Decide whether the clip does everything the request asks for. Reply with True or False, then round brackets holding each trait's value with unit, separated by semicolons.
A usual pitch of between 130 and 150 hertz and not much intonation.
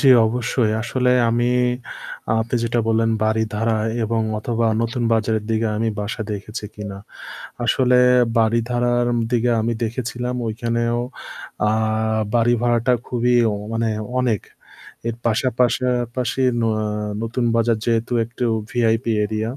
False (115 Hz; 1.6 semitones)